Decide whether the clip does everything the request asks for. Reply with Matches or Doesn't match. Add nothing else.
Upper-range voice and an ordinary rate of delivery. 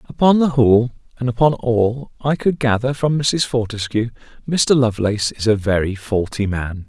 Doesn't match